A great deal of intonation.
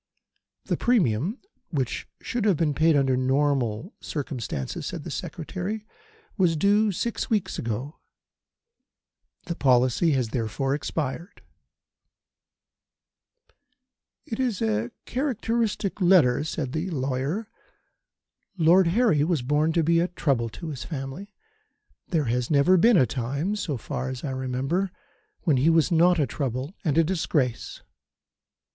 Yes: wide, 5.8 semitones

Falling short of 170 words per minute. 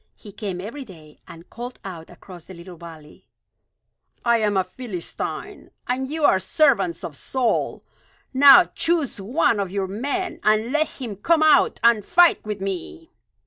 Yes: average, 160 wpm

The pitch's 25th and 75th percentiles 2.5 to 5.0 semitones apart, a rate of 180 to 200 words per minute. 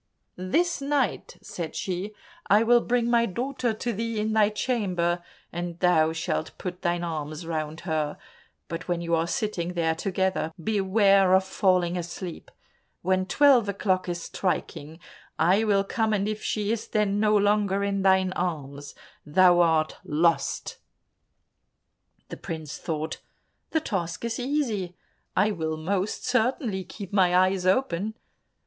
No: average, 3.8 semitones; average, 145 wpm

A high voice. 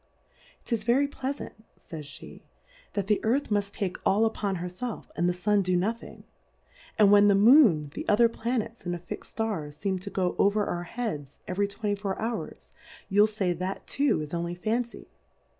Yes: high, 205 Hz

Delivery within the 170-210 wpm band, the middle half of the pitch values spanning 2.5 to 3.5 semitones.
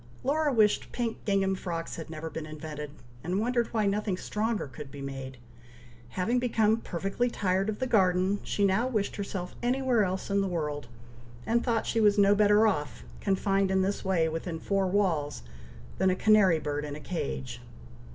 No: average, 180 wpm; average, 4.8 semitones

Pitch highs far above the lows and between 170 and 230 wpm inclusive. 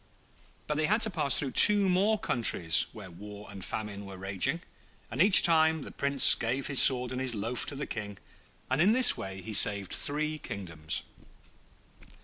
Yes: wide, 7.7 semitones; average, 180 wpm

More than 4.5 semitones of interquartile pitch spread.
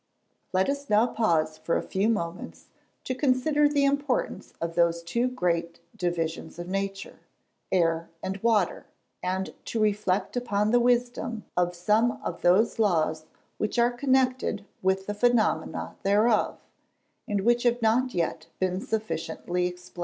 Yes: average, 5.3 semitones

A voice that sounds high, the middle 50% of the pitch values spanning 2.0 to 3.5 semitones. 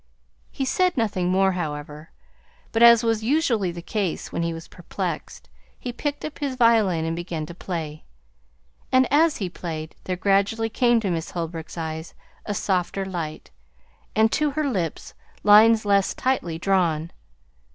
No: high, 195 Hz; wide, 5.5 semitones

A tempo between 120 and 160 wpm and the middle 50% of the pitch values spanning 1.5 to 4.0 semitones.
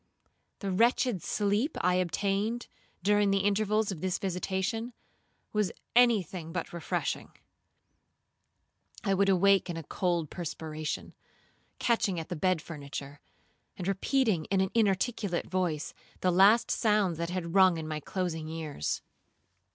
Yes: slow, 135 wpm; average, 3.5 semitones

